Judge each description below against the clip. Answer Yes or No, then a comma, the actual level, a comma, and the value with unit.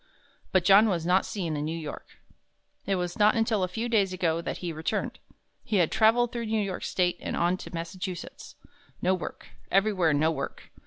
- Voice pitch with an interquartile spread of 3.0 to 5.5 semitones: Yes, average, 3.8 semitones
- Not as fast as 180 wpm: No, average, 195 wpm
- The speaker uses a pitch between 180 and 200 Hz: Yes, medium, 185 Hz